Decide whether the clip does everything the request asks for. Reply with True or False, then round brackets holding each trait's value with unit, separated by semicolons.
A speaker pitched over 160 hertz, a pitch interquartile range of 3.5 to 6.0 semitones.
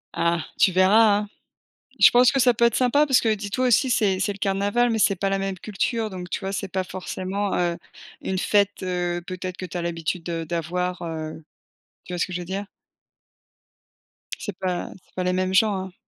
False (190 Hz; 2.6 semitones)